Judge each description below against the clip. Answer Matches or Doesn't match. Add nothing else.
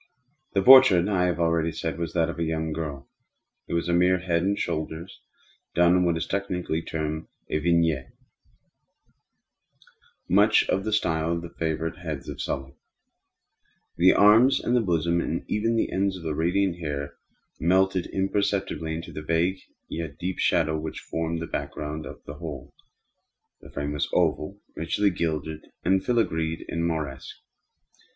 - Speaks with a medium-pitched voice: Doesn't match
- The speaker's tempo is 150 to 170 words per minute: Matches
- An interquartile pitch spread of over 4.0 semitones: Doesn't match